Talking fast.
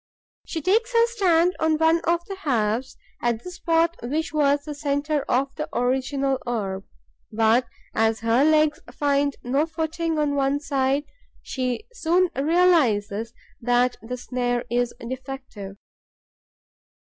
No: slow, 135 wpm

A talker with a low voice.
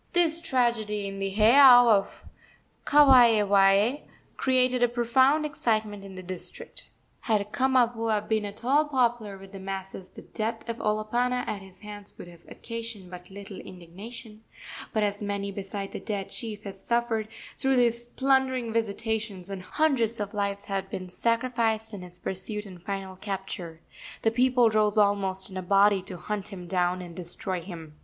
No: high, 210 Hz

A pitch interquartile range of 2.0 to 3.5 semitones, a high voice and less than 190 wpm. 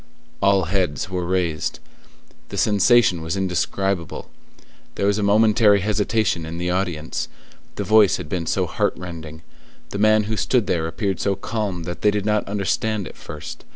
No: average, 3.2 semitones; very low, 95 Hz; average, 165 wpm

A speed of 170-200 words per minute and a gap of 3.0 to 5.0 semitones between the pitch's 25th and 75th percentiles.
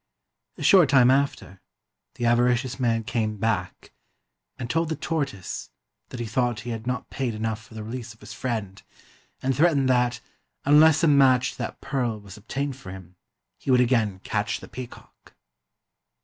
Yes: average, 175 wpm; average, 3.3 semitones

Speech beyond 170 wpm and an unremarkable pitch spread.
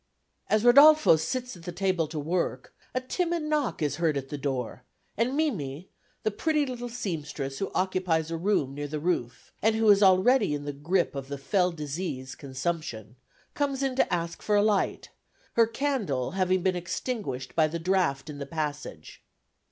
No: average, 180 wpm; wide, 7.2 semitones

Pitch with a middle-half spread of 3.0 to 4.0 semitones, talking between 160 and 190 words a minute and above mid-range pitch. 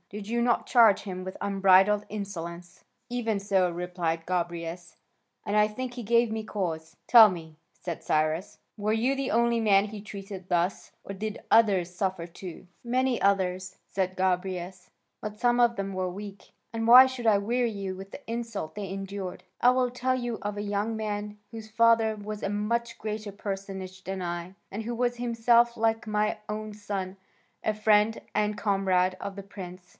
Yes: average, 3.3 semitones; average, 180 wpm; high, 205 Hz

